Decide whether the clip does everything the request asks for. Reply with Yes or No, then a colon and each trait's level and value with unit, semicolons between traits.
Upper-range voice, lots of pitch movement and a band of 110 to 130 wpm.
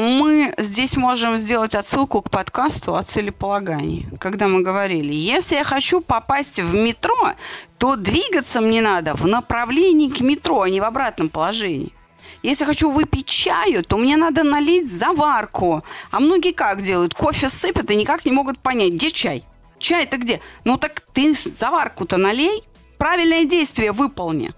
No: very high, 270 Hz; wide, 6.9 semitones; average, 155 wpm